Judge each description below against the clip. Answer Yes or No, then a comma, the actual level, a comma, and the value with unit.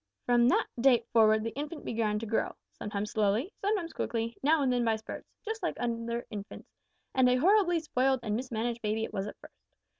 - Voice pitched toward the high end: Yes, high, 235 Hz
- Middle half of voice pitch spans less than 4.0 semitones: Yes, average, 3.5 semitones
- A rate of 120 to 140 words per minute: No, average, 200 wpm